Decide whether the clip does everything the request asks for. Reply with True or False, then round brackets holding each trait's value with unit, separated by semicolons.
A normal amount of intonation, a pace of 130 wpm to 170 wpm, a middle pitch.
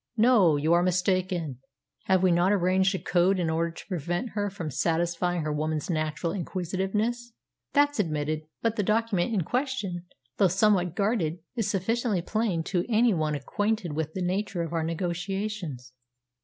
True (3.9 semitones; 160 wpm; 180 Hz)